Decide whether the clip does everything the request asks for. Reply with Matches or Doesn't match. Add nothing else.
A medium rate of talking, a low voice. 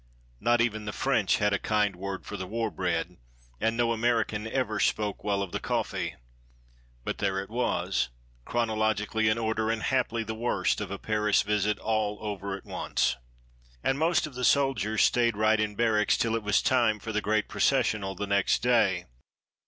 Matches